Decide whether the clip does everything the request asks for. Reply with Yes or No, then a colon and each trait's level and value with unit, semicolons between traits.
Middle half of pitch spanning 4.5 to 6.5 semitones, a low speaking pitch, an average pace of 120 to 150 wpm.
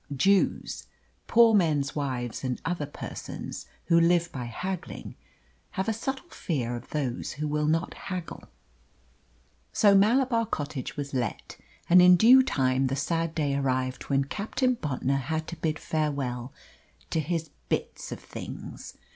No: average, 5.2 semitones; medium, 155 Hz; average, 145 wpm